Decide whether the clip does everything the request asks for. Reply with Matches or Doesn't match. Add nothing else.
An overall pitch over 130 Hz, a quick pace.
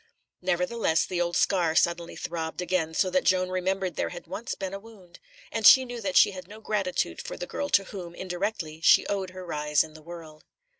Matches